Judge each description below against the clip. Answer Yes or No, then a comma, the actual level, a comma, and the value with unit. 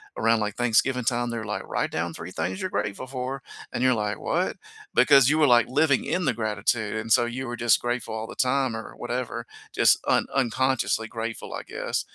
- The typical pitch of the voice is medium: No, low, 120 Hz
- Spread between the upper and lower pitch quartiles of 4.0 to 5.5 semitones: No, average, 2.9 semitones